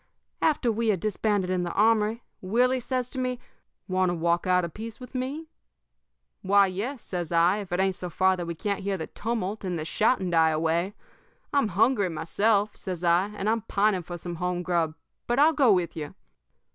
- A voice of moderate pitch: No, high, 195 Hz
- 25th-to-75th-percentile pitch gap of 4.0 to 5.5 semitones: Yes, average, 4.4 semitones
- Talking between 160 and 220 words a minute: Yes, average, 200 wpm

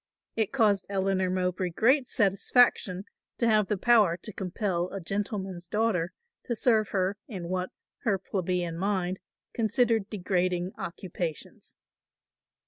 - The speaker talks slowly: Yes, slow, 125 wpm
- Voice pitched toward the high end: Yes, high, 195 Hz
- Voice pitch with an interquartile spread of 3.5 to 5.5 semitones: No, average, 2.9 semitones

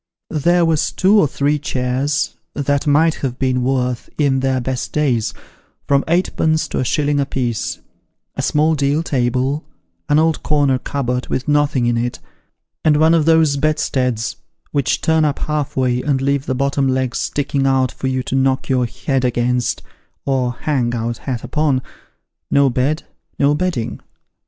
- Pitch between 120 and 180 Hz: Yes, medium, 140 Hz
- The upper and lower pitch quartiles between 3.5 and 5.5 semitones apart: No, average, 2.8 semitones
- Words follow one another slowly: No, average, 165 wpm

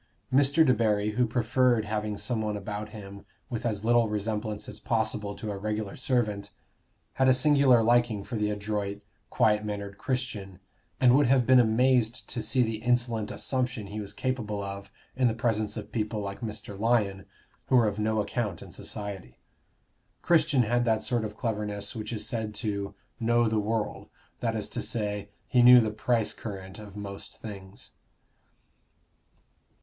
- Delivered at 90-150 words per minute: No, average, 165 wpm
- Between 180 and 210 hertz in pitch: No, low, 110 Hz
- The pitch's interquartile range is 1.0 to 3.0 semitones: Yes, average, 2.7 semitones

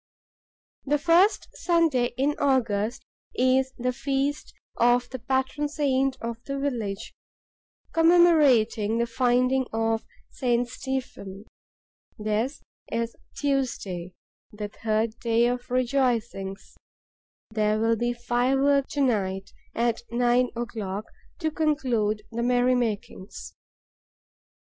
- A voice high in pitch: Yes, high, 245 Hz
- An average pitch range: Yes, average, 3.2 semitones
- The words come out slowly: Yes, slow, 105 wpm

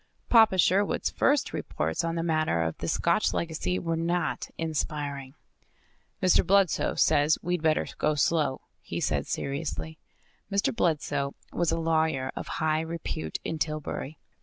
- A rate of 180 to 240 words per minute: No, average, 140 wpm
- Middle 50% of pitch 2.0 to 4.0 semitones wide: Yes, narrow, 2.6 semitones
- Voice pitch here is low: No, medium, 160 Hz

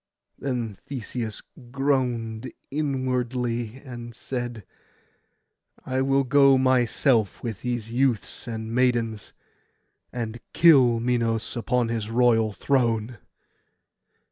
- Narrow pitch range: Yes, narrow, 2.3 semitones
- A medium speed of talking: No, slow, 90 wpm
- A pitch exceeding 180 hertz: No, low, 120 Hz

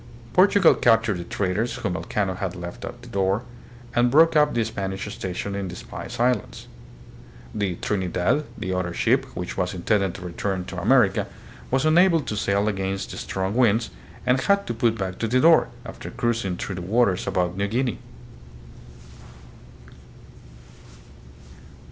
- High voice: No, low, 105 Hz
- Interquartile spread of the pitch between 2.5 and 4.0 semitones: No, average, 4.5 semitones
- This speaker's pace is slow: No, average, 155 wpm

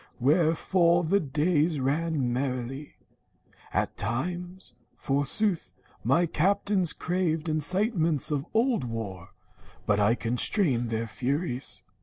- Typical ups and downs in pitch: No, wide, 5.9 semitones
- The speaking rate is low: Yes, slow, 100 wpm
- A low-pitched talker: No, medium, 155 Hz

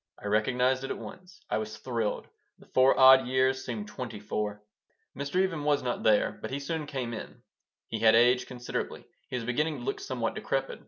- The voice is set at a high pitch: No, low, 130 Hz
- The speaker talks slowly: No, average, 200 wpm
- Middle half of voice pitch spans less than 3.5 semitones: No, average, 3.9 semitones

